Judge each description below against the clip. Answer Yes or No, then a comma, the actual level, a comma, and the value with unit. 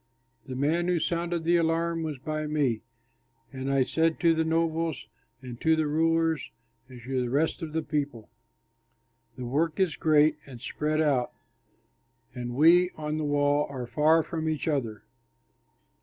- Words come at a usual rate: Yes, average, 160 wpm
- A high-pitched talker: No, medium, 155 Hz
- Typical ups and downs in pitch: Yes, average, 3.1 semitones